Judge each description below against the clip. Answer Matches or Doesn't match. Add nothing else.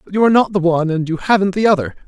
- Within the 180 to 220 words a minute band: Doesn't match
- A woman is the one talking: Doesn't match